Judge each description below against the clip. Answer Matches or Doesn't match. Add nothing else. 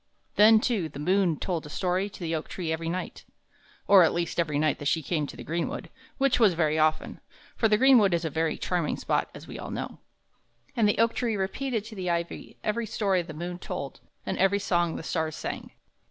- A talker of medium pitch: Matches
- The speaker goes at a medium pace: Doesn't match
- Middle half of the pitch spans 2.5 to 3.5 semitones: Doesn't match